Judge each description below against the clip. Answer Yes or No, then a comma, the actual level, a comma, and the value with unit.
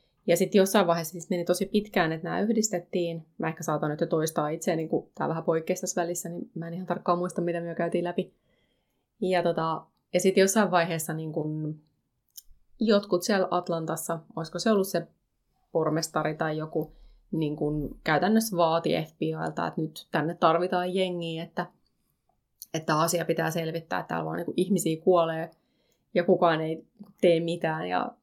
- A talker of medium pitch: Yes, medium, 170 Hz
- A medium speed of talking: No, fast, 170 wpm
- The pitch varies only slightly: Yes, narrow, 2.0 semitones